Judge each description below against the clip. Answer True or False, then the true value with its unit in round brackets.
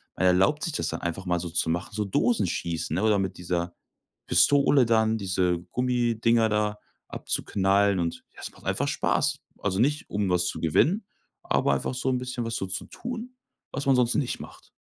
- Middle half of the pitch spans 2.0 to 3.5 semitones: False (5.6 semitones)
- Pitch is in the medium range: False (105 Hz)